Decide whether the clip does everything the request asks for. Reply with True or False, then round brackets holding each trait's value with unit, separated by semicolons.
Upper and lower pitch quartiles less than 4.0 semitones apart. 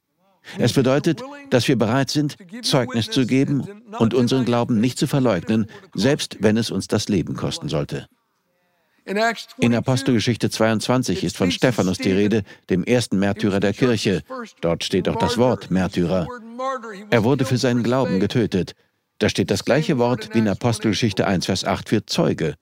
False (5.2 semitones)